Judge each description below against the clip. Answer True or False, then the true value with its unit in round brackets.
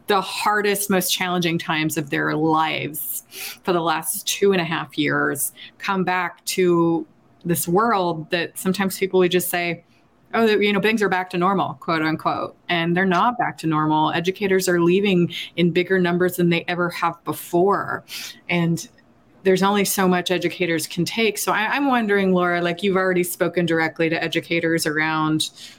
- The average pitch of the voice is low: False (175 Hz)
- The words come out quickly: False (175 wpm)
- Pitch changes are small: True (2.3 semitones)